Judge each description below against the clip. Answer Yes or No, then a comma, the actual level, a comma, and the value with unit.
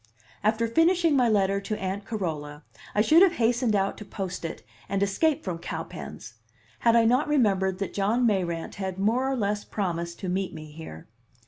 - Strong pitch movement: No, average, 4.0 semitones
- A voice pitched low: No, high, 200 Hz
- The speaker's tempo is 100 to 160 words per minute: No, average, 185 wpm